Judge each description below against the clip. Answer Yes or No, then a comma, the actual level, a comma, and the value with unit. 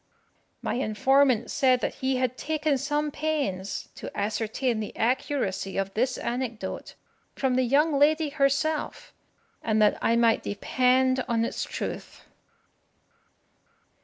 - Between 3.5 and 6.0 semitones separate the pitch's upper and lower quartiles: Yes, average, 4.0 semitones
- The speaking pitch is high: Yes, very high, 255 Hz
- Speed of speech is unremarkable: No, slow, 125 wpm